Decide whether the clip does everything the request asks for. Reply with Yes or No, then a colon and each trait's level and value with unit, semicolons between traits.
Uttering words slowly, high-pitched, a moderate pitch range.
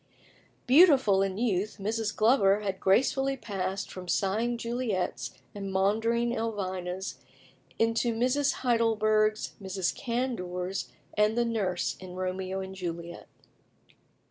Yes: slow, 110 wpm; high, 210 Hz; average, 3.6 semitones